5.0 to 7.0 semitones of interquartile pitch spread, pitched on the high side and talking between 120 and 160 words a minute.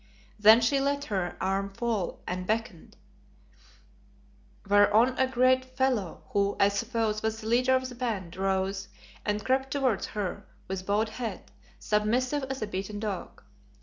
No: average, 4.3 semitones; high, 215 Hz; average, 150 wpm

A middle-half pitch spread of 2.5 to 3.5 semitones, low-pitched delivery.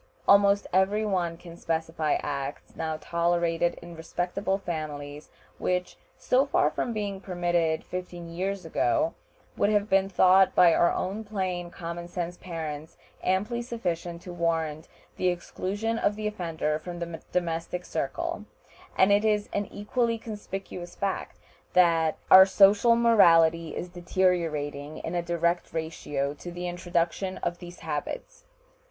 No: average, 3.0 semitones; medium, 175 Hz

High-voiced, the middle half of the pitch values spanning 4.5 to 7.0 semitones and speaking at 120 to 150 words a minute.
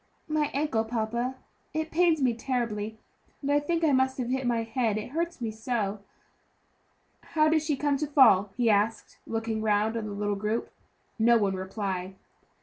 No: high, 235 Hz; average, 4.8 semitones; average, 175 wpm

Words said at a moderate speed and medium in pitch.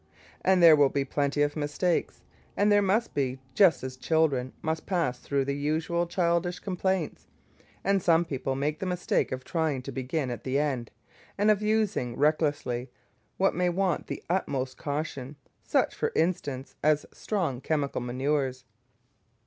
Yes: average, 155 wpm; medium, 150 Hz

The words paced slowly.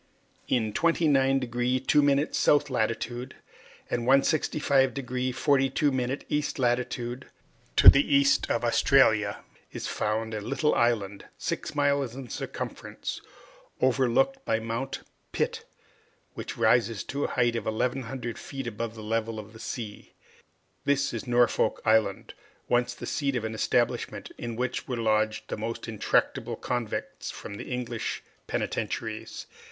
Yes: slow, 130 wpm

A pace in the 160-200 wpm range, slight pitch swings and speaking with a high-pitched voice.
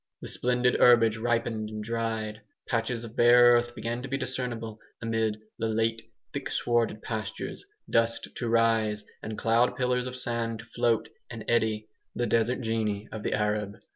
No: average, 165 wpm; narrow, 1.5 semitones; low, 115 Hz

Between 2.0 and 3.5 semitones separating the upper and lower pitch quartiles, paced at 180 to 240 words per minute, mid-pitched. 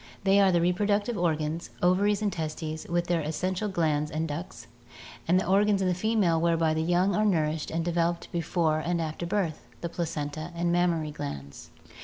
Yes: average, 2.8 semitones; average, 185 wpm; medium, 170 Hz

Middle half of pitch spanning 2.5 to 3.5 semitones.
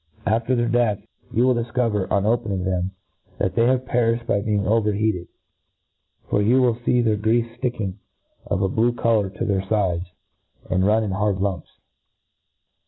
Yes: average, 3.2 semitones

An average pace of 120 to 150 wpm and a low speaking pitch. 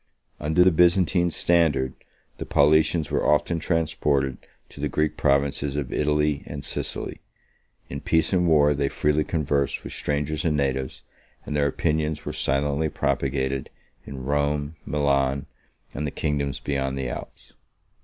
Yes: average, 145 wpm; very low, 75 Hz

